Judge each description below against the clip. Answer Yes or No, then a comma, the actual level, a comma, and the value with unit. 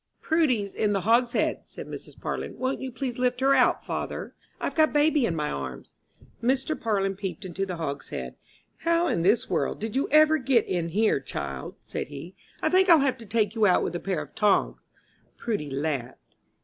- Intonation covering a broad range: Yes, wide, 7.4 semitones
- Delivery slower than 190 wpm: No, average, 195 wpm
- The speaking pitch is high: Yes, high, 215 Hz